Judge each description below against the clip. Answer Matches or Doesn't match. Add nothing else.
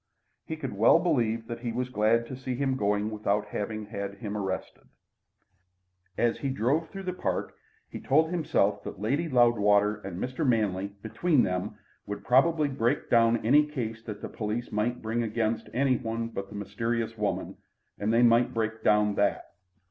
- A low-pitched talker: Matches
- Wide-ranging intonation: Doesn't match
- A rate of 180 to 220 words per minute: Doesn't match